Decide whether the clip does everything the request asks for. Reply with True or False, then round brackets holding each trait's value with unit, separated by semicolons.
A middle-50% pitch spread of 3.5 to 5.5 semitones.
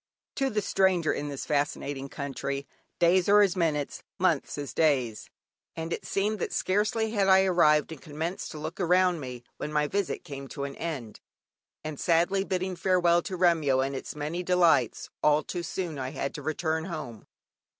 True (4.4 semitones)